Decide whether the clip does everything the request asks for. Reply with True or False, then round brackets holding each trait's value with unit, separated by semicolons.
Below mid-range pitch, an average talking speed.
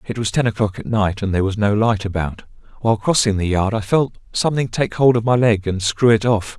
False (110 Hz; 255 wpm)